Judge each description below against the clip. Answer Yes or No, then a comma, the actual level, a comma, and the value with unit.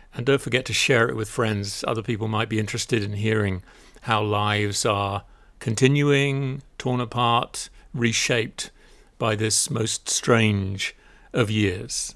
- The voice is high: No, low, 110 Hz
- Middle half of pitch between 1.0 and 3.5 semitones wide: Yes, average, 2.8 semitones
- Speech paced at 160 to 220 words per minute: No, average, 140 wpm